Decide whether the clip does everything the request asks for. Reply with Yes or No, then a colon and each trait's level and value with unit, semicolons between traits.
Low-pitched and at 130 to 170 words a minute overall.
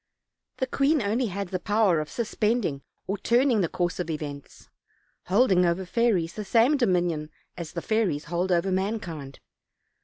No: high, 190 Hz; average, 155 wpm